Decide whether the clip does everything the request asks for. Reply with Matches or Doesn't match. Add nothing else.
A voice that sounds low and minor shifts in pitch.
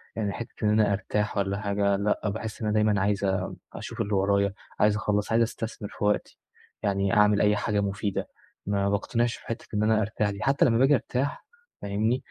Matches